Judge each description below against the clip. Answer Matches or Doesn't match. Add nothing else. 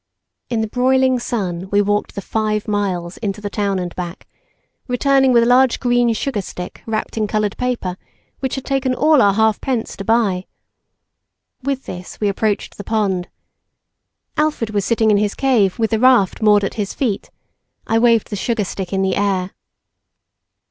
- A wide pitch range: Doesn't match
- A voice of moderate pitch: Doesn't match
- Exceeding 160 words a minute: Matches